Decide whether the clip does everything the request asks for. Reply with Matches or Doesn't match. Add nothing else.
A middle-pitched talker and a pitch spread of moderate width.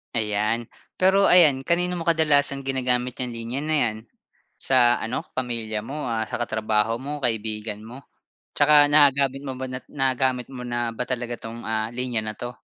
Doesn't match